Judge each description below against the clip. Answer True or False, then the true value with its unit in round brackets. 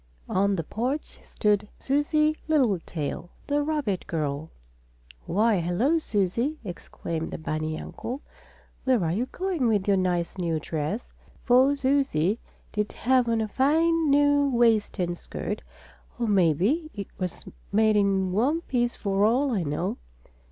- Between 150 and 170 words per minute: False (140 wpm)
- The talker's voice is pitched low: False (215 Hz)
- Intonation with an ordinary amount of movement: False (7.1 semitones)